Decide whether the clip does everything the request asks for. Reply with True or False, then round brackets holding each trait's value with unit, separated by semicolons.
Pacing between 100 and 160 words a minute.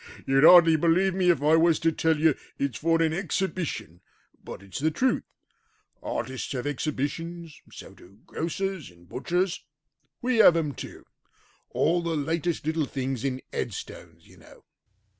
True (155 wpm)